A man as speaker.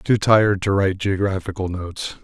Yes: male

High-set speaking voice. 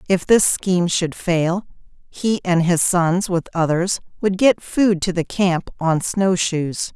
No: medium, 180 Hz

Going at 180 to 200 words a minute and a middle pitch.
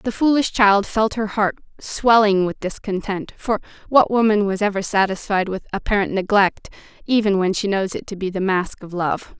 No: average, 185 wpm; high, 200 Hz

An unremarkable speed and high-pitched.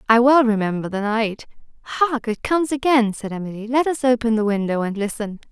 Yes: average, 195 wpm; high, 230 Hz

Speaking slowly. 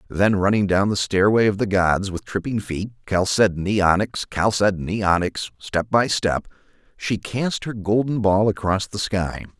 No: average, 165 wpm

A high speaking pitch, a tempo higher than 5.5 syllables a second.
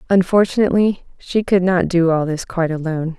No: medium, 180 Hz; 5.9 syllables/s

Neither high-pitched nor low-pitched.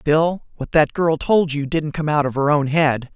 Yes: medium, 150 Hz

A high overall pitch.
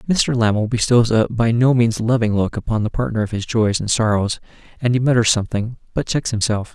No: low, 115 Hz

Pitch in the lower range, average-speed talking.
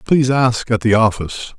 Yes: low, 115 Hz; average, 190 wpm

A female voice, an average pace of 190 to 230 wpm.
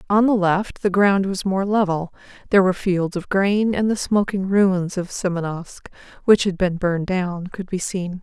Yes: female; average, 195 wpm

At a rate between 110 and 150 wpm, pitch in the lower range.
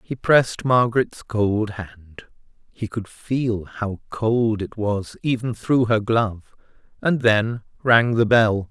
Yes: average, 145 wpm; low, 110 Hz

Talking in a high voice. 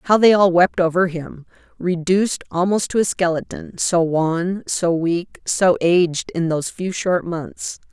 No: medium, 175 Hz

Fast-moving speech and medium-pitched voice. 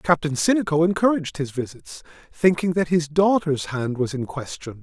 No: average, 160 wpm; medium, 160 Hz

